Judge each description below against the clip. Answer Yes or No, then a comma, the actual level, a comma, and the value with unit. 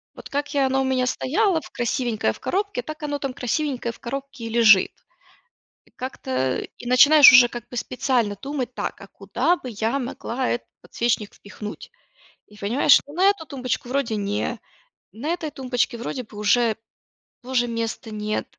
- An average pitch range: Yes, average, 3.4 semitones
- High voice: Yes, very high, 250 Hz